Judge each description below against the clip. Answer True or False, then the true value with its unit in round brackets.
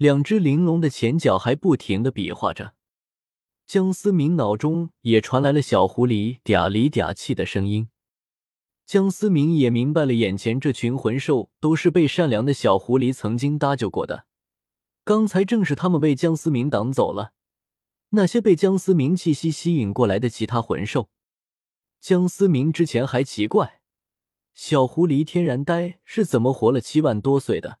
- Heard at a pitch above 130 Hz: True (140 Hz)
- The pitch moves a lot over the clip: True (6.8 semitones)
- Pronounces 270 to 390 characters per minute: False (250 characters per minute)